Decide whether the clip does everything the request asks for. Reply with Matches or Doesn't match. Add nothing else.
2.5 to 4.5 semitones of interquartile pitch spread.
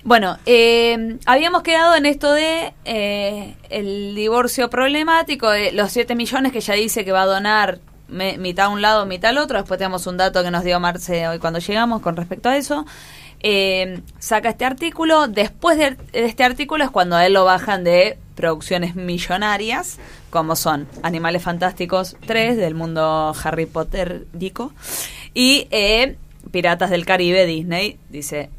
Doesn't match